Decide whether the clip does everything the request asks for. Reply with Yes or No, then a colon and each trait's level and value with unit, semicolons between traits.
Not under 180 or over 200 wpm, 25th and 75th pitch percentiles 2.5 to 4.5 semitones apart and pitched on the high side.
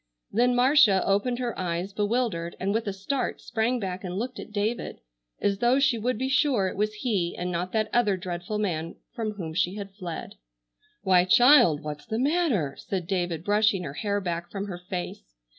No: average, 190 wpm; average, 4.9 semitones; high, 200 Hz